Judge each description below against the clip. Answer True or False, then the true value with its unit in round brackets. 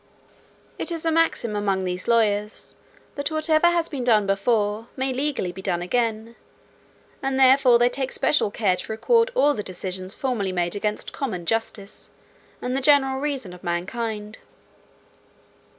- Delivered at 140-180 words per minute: True (150 wpm)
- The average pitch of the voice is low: False (230 Hz)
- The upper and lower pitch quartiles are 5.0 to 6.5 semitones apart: True (5.3 semitones)